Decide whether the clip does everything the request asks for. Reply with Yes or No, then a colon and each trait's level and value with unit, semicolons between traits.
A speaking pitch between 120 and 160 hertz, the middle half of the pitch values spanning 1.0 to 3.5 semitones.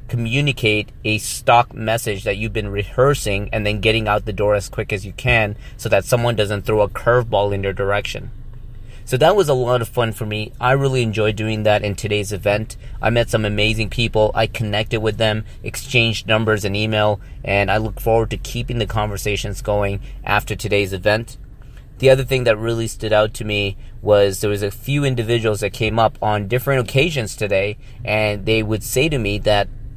No: low, 110 Hz; narrow, 2.4 semitones